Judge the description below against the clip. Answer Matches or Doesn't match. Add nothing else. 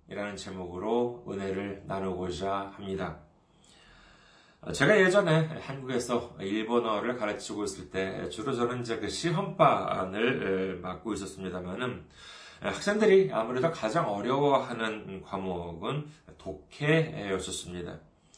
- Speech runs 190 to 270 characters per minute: Matches